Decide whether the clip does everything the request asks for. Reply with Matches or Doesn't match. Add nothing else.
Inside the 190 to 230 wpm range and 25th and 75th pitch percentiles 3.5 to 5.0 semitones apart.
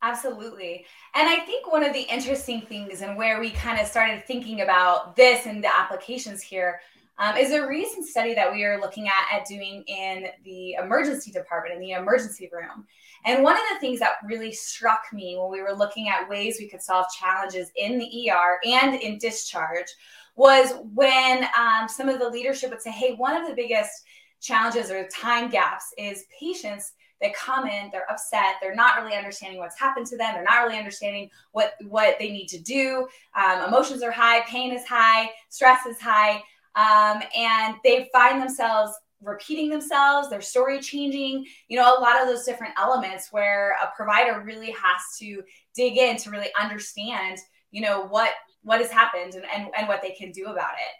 Matches